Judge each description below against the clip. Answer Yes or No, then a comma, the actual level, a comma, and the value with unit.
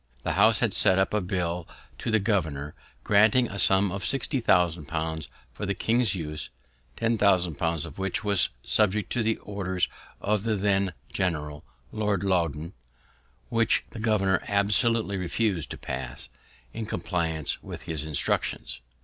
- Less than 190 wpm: Yes, average, 155 wpm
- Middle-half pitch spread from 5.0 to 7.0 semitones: No, average, 4.1 semitones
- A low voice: Yes, very low, 95 Hz